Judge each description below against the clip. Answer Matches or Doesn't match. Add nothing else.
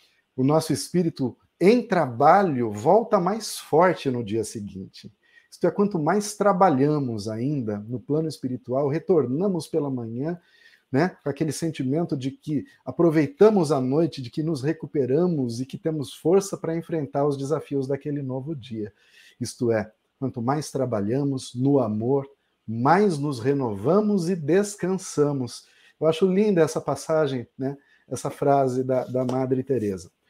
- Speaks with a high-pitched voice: Doesn't match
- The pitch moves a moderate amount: Matches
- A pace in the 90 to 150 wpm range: Matches